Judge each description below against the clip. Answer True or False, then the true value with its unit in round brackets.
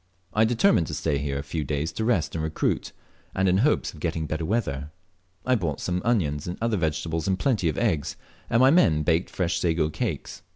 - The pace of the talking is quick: True (210 wpm)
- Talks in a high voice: False (85 Hz)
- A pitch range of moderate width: False (5.7 semitones)